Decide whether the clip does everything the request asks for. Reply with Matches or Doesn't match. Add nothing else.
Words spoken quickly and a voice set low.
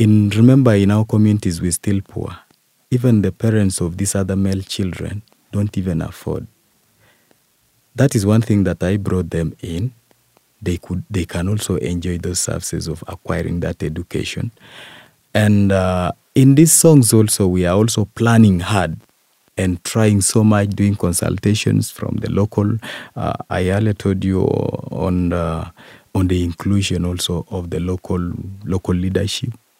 Doesn't match